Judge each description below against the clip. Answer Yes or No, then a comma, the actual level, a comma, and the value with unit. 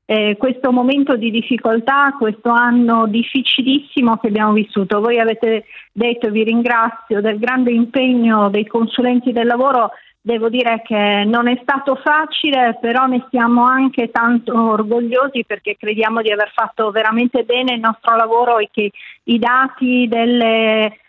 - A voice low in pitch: No, high, 235 Hz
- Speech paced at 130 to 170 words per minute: Yes, average, 145 wpm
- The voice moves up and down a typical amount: No, narrow, 2.0 semitones